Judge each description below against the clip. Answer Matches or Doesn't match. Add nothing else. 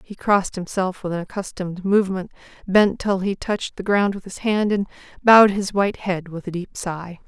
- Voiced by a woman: Matches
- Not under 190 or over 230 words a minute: Matches